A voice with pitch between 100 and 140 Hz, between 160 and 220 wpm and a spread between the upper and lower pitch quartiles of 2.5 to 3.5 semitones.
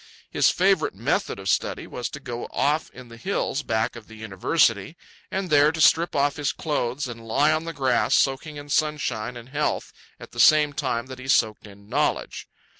No: low, 135 Hz; average, 195 wpm; average, 4.3 semitones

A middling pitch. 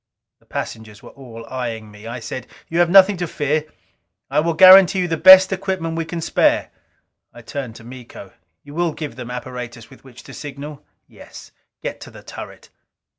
Yes: medium, 145 Hz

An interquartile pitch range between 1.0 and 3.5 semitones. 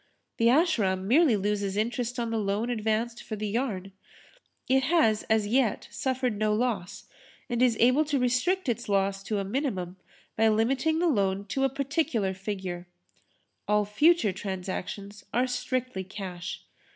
No: average, 4.3 semitones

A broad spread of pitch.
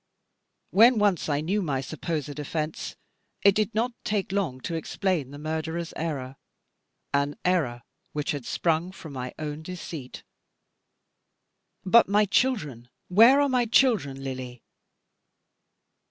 Yes: wide, 6.0 semitones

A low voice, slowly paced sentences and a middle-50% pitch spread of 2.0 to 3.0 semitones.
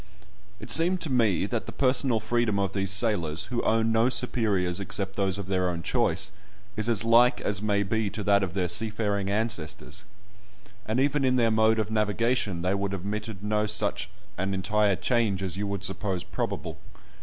No: low, 105 Hz; average, 185 wpm; average, 2.7 semitones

